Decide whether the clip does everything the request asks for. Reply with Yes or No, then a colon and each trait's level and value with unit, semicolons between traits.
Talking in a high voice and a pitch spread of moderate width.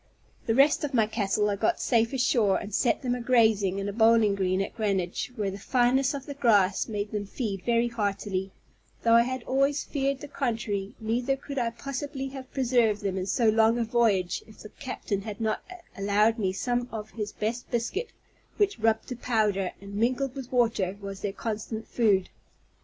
Yes: high, 225 Hz; average, 3.6 semitones